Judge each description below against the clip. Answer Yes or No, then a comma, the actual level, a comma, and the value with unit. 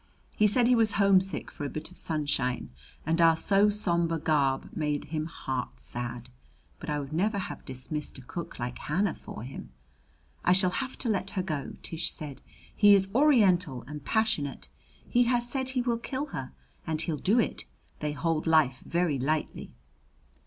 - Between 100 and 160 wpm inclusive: No, average, 180 wpm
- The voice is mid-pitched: Yes, medium, 165 Hz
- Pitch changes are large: Yes, wide, 6.0 semitones